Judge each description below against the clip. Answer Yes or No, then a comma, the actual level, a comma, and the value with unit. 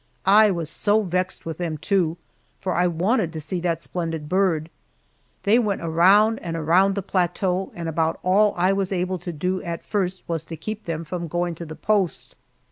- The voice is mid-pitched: Yes, medium, 180 Hz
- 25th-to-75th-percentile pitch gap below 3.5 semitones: Yes, average, 2.8 semitones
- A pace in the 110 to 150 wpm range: No, average, 195 wpm